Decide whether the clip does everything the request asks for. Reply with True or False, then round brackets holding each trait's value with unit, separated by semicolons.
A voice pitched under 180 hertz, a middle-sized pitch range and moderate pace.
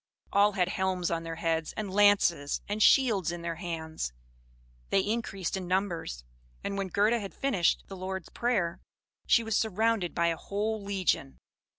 False (190 Hz; 3.4 semitones; 165 wpm)